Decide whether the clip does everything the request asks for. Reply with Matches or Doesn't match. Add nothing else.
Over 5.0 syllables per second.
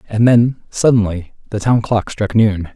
Doesn't match